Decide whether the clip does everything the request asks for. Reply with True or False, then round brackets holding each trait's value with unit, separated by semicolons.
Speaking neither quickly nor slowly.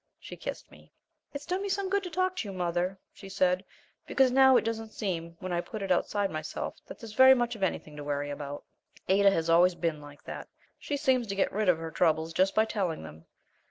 False (230 wpm)